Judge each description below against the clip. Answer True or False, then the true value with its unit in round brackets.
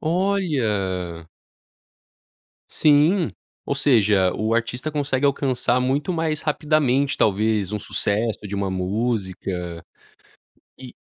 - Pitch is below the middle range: True (120 Hz)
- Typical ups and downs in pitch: False (6.7 semitones)